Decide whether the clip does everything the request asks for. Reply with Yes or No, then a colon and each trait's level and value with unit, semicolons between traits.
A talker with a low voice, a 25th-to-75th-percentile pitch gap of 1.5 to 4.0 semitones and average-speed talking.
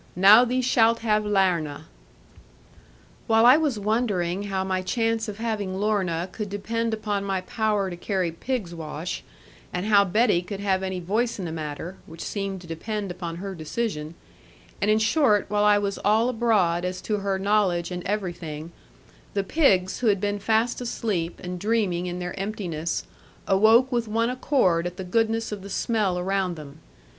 No: high, 200 Hz; average, 3.6 semitones; average, 175 wpm